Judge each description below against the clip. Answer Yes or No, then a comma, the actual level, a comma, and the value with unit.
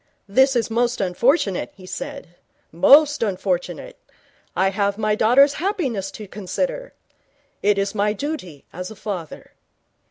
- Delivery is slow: Yes, slow, 130 wpm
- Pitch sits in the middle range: No, high, 210 Hz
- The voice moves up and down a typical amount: No, wide, 6.1 semitones